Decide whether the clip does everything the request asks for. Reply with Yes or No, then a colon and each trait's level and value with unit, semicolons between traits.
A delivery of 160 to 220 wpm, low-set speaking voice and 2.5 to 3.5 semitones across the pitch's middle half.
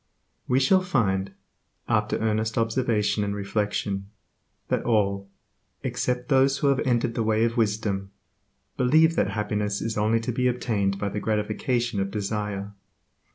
No: average, 145 wpm; low, 110 Hz; average, 3.2 semitones